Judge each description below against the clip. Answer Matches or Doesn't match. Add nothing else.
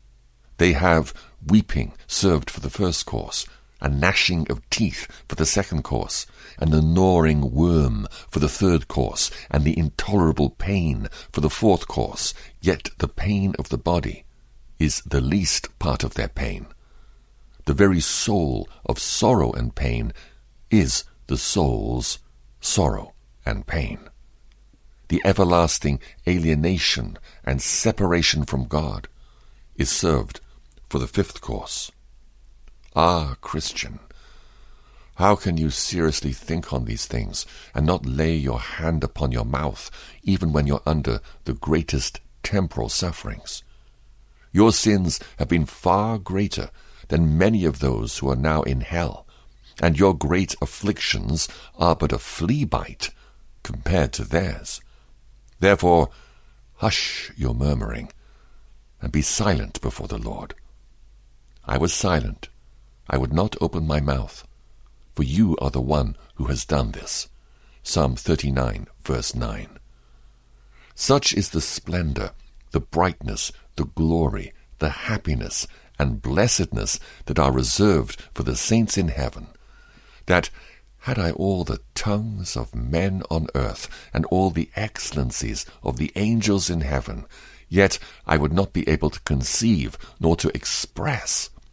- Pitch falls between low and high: Doesn't match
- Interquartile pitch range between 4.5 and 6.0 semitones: Matches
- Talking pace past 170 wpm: Doesn't match